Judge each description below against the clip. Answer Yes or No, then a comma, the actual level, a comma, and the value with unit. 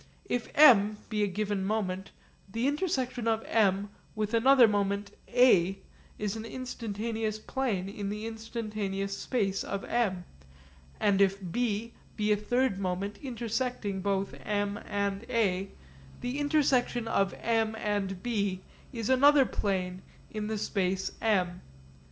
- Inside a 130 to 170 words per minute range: Yes, slow, 135 wpm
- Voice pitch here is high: Yes, high, 210 Hz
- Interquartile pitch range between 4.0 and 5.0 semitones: No, average, 2.9 semitones